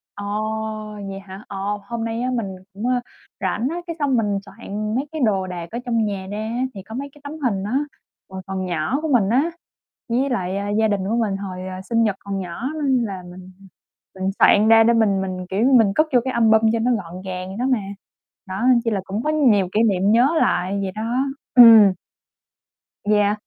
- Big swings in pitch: No, average, 3.5 semitones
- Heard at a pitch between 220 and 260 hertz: No, high, 210 Hz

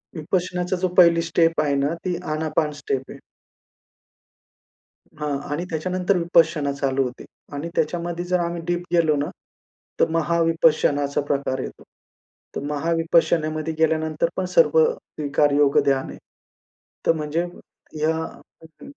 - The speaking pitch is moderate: Yes, medium, 160 Hz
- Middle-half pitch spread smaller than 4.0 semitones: Yes, narrow, 2.6 semitones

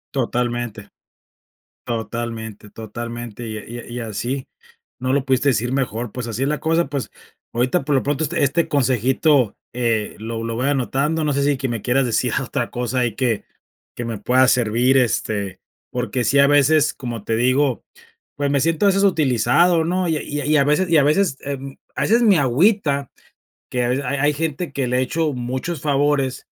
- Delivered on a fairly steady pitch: No, average, 3.5 semitones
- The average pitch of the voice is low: Yes, low, 130 Hz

